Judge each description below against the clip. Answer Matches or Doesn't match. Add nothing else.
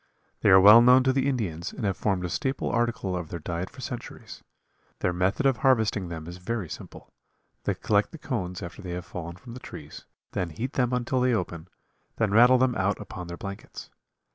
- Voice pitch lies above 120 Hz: Doesn't match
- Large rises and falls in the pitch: Matches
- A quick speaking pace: Matches